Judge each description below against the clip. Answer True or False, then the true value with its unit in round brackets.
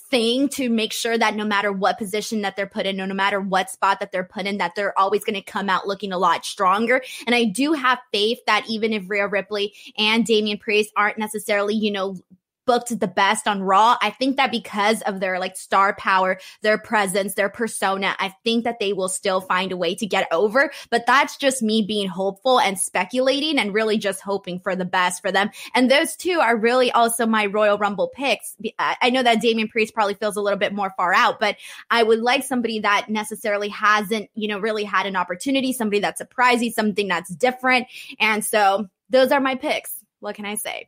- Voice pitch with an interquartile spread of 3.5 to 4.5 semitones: False (2.8 semitones)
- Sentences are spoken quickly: True (220 wpm)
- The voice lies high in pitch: True (210 Hz)